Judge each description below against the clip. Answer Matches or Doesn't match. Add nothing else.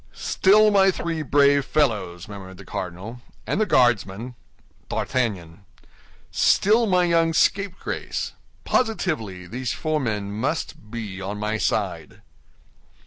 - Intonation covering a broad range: Matches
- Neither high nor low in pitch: Doesn't match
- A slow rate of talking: Matches